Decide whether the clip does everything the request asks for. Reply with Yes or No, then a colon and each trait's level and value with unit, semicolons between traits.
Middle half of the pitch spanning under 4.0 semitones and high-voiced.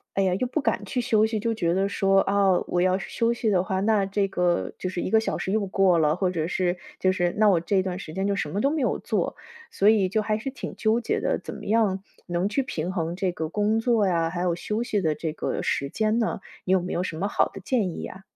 Yes: average, 3.3 semitones; high, 195 Hz